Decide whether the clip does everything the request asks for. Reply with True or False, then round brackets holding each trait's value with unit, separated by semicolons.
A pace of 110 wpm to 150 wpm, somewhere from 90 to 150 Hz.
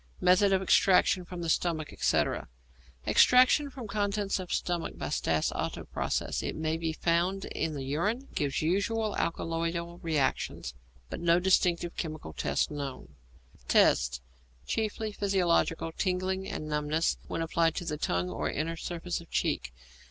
False (145 wpm; 170 Hz)